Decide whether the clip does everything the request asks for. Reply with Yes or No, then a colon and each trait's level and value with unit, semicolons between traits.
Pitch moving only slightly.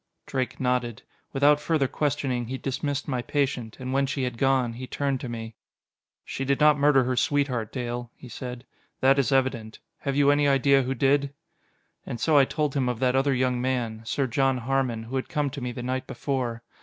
Yes: narrow, 2.2 semitones